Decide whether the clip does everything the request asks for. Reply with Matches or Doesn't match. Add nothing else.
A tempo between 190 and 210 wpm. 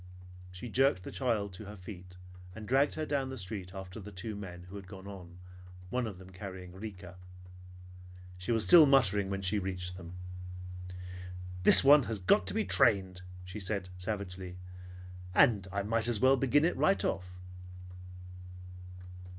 Doesn't match